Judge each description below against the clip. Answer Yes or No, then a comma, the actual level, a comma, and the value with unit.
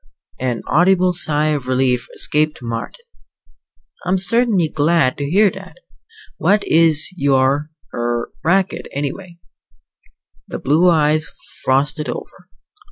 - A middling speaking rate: No, slow, 110 wpm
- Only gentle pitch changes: No, average, 4.9 semitones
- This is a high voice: No, medium, 155 Hz